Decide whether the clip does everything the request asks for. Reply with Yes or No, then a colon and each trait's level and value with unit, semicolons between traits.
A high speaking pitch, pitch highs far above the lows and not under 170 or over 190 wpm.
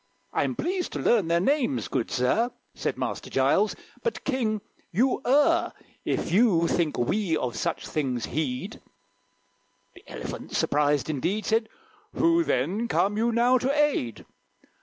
No: high, 210 Hz; wide, 9.0 semitones; average, 140 wpm